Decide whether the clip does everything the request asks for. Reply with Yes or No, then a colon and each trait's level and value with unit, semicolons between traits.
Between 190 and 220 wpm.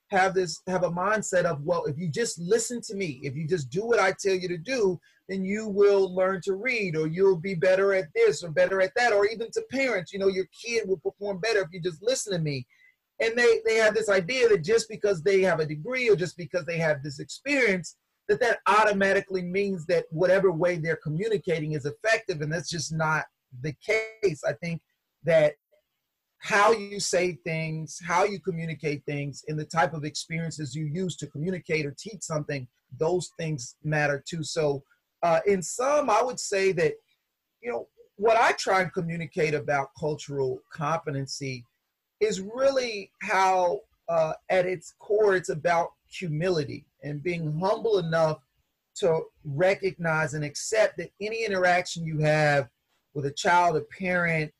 No: average, 180 wpm